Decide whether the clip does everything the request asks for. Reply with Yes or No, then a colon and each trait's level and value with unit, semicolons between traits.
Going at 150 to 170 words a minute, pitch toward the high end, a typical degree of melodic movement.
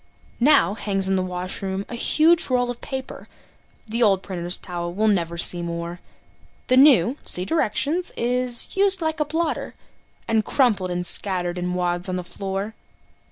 No: average, 160 wpm; high, 200 Hz; wide, 6.1 semitones